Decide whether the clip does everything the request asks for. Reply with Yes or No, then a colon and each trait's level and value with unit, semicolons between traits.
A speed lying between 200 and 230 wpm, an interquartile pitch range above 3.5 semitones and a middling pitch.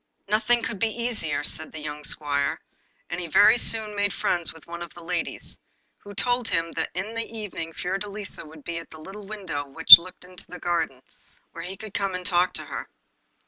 Yes: fast, 205 wpm; average, 4.1 semitones; medium, 180 Hz